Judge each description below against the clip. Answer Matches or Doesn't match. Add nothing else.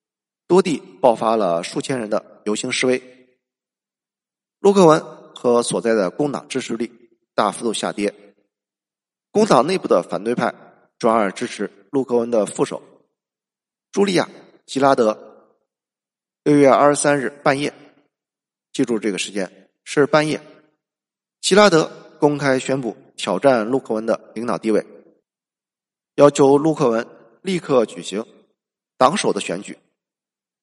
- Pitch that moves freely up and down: Doesn't match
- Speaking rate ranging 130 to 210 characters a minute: Matches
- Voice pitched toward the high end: Doesn't match